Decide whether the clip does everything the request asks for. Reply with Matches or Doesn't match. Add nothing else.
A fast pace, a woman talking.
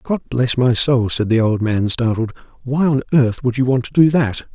Doesn't match